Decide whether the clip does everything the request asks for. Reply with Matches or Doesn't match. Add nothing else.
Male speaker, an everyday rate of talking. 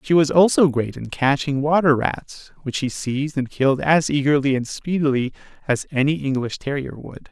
Matches